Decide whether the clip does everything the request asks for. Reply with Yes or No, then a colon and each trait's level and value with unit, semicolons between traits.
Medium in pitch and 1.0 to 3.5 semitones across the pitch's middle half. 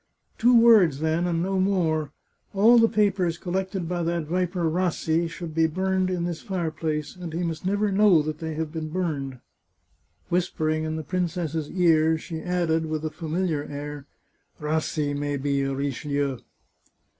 Yes: medium, 165 Hz; average, 2.8 semitones